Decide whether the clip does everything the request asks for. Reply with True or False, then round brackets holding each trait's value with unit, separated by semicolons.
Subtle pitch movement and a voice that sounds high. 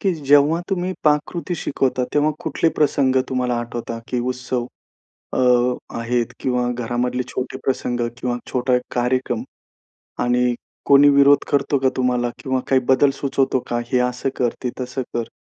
False (2.3 semitones; 130 Hz)